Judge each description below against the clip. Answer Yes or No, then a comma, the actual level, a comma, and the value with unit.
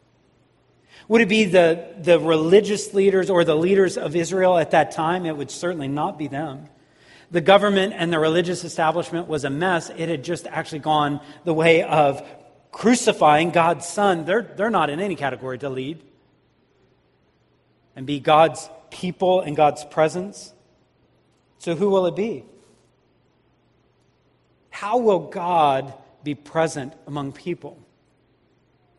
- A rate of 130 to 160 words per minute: Yes, average, 140 wpm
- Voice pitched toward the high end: No, medium, 165 Hz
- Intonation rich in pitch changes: No, average, 3.8 semitones